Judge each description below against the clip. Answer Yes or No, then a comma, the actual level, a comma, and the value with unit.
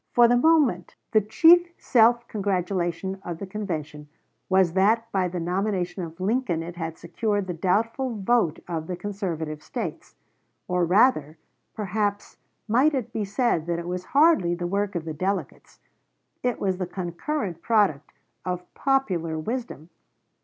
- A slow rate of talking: No, average, 150 wpm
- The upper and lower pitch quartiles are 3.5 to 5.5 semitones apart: Yes, average, 4.6 semitones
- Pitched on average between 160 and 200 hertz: Yes, high, 190 Hz